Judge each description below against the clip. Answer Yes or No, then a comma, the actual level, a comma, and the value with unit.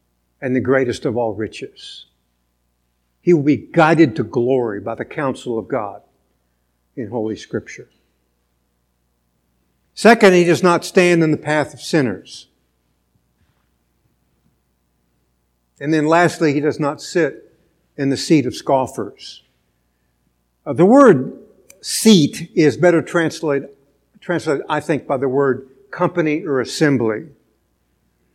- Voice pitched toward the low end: Yes, low, 125 Hz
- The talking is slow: Yes, slow, 125 wpm